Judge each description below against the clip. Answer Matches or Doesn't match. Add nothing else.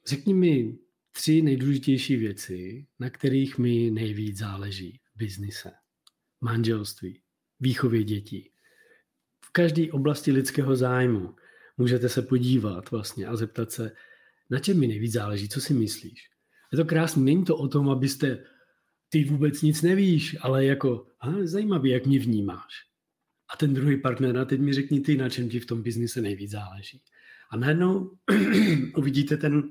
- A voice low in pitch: Matches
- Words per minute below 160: Matches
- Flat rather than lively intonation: Doesn't match